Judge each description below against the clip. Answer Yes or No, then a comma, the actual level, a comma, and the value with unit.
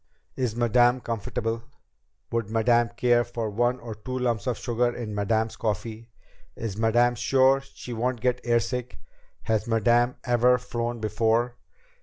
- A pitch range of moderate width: No, narrow, 1.6 semitones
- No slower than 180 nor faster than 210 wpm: No, average, 140 wpm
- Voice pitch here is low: Yes, low, 120 Hz